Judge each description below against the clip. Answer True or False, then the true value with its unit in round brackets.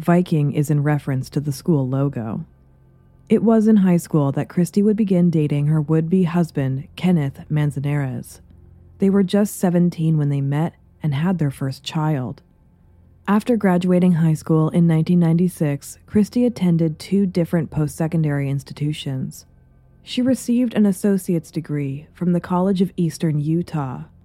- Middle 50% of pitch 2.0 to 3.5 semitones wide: False (4.1 semitones)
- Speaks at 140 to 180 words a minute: True (150 wpm)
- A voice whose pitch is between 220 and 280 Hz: False (160 Hz)